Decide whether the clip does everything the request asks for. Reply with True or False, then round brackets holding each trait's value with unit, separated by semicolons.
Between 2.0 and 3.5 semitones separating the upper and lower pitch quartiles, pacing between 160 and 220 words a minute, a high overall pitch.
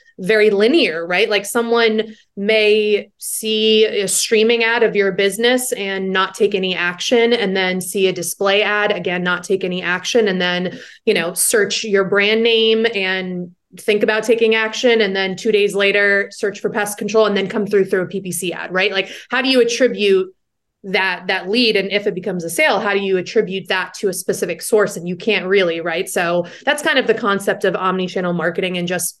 True (2.8 semitones; 205 wpm; 200 Hz)